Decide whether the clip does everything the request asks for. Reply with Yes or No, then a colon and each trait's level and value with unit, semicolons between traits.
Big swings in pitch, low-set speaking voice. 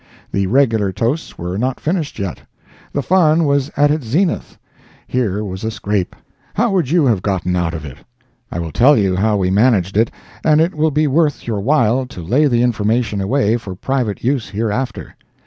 Yes: wide, 6.4 semitones; low, 115 Hz